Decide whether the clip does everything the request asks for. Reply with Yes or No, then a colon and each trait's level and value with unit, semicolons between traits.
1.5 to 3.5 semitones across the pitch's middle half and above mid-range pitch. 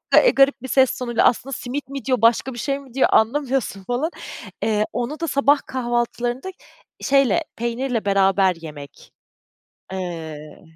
No: average, 4.6 semitones; high, 245 Hz